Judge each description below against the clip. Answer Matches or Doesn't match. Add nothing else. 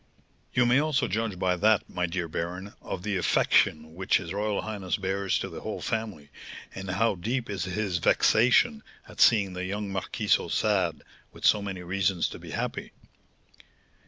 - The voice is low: Matches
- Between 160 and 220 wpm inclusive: Matches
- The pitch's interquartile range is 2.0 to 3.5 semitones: Matches